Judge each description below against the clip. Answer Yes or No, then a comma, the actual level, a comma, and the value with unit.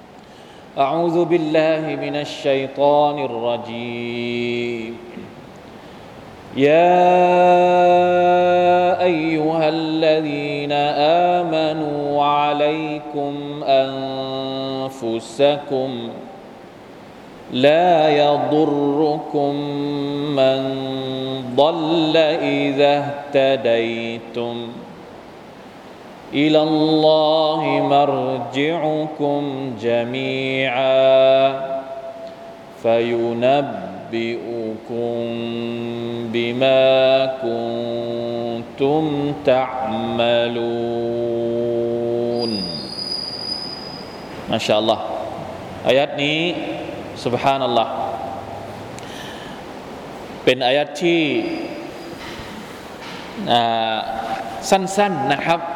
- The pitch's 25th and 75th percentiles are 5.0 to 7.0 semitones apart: No, average, 4.6 semitones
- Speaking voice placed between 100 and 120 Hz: No, low, 135 Hz